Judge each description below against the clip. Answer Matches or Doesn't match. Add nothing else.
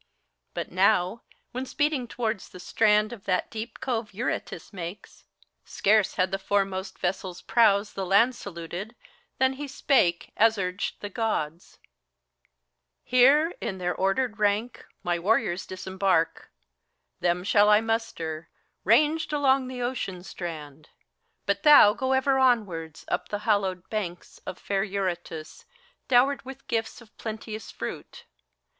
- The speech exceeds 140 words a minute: Doesn't match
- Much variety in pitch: Doesn't match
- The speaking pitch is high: Matches